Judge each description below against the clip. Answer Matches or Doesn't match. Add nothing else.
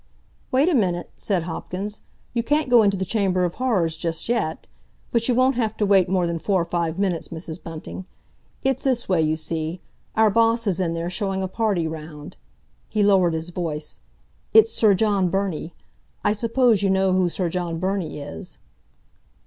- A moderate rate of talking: Matches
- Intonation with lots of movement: Doesn't match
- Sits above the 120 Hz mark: Matches